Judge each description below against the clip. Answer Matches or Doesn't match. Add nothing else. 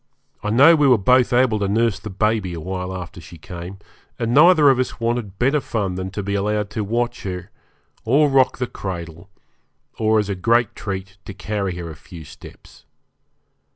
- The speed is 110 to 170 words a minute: Doesn't match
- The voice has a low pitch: Matches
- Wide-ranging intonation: Doesn't match